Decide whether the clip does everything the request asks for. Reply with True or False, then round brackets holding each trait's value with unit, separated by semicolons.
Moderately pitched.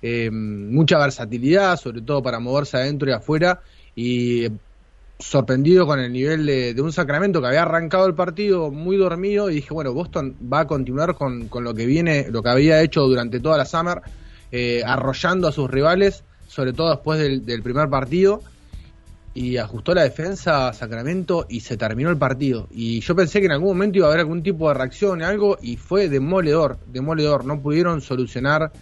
True (145 Hz)